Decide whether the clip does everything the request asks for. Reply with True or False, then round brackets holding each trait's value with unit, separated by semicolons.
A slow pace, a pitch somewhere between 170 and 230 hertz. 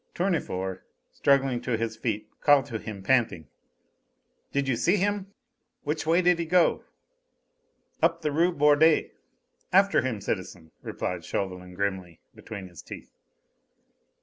False (130 wpm; 130 Hz)